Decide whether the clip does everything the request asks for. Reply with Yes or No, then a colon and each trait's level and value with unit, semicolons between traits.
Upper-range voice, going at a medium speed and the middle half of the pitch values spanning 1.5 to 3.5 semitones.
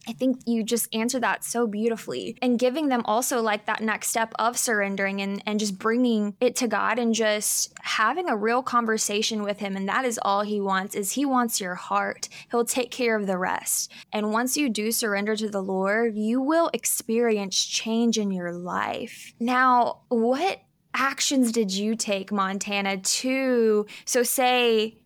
Yes: high, 225 Hz; average, 180 wpm; average, 2.9 semitones